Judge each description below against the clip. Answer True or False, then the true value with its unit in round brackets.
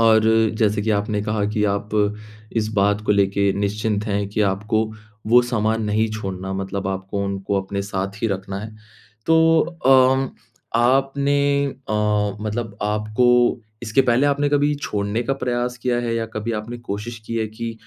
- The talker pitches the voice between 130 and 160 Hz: False (110 Hz)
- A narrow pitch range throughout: False (3.1 semitones)